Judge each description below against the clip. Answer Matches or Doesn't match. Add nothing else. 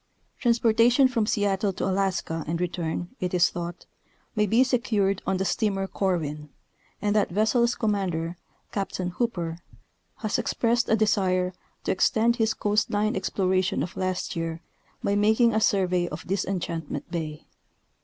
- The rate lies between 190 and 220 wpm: Doesn't match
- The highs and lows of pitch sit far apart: Doesn't match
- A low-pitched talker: Doesn't match